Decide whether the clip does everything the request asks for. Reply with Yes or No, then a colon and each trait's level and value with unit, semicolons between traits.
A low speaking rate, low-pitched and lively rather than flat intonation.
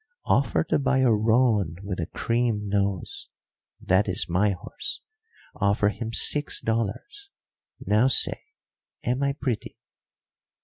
No: slow, 125 wpm; low, 110 Hz; average, 4.2 semitones